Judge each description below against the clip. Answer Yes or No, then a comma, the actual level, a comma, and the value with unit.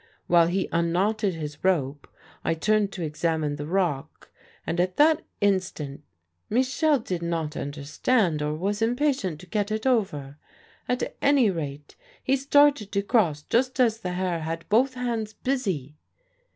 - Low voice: No, medium, 185 Hz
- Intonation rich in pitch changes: Yes, wide, 6.6 semitones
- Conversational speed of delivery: Yes, average, 150 wpm